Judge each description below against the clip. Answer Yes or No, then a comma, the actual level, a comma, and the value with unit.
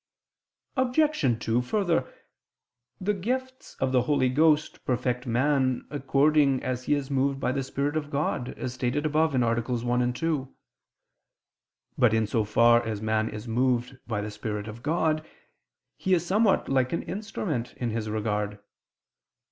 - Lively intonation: No, average, 4.5 semitones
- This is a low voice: Yes, low, 130 Hz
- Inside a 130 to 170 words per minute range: Yes, average, 150 wpm